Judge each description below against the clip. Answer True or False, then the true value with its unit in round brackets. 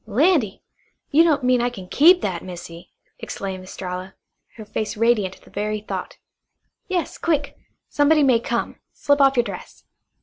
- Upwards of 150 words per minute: True (160 wpm)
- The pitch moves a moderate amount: False (6.8 semitones)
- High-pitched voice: True (235 Hz)